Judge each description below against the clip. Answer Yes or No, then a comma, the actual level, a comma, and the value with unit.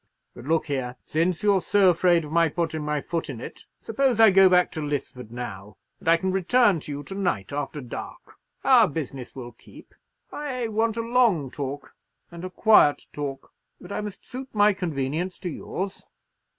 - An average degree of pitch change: No, wide, 6.1 semitones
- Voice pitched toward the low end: No, medium, 170 Hz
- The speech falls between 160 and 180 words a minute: No, average, 190 wpm